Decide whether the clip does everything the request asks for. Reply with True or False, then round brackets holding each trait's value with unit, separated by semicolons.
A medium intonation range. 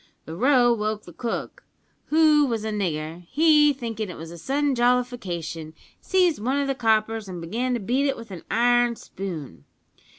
False (6.3 semitones)